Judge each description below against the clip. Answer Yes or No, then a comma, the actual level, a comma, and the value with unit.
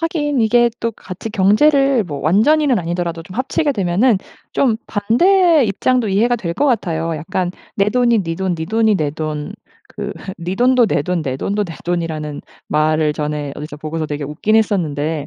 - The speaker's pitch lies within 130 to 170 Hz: No, high, 190 Hz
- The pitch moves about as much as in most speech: No, wide, 7.0 semitones